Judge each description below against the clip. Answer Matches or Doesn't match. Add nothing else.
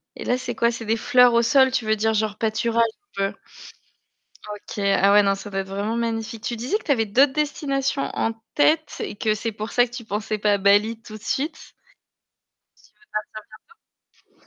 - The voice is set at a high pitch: Matches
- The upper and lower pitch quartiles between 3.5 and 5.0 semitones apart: Doesn't match